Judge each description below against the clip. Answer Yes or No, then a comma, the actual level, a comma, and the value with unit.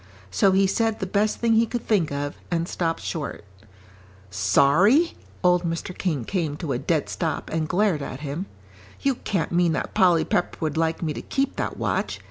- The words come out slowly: No, average, 190 wpm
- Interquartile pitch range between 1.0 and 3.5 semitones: No, average, 4.5 semitones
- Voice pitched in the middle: Yes, medium, 175 Hz